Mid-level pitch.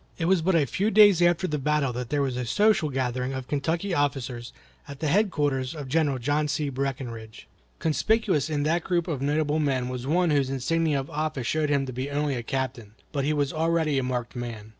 Yes: medium, 145 Hz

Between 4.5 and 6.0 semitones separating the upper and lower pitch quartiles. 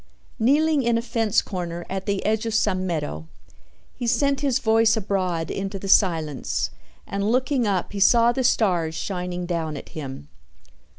Yes: average, 4.8 semitones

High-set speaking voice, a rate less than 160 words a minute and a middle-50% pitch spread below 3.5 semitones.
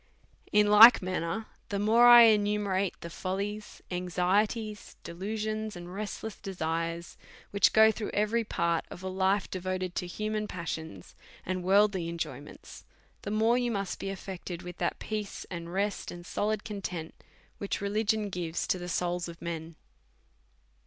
Yes: high, 195 Hz; average, 150 wpm; average, 3.1 semitones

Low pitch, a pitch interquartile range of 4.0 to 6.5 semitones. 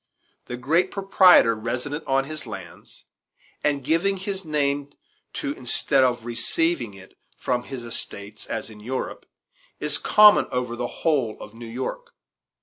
Yes: low, 130 Hz; average, 5.2 semitones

